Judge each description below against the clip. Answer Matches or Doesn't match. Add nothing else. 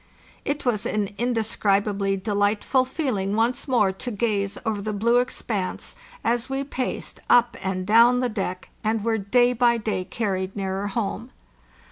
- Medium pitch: Doesn't match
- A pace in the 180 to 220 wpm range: Doesn't match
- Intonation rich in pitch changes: Doesn't match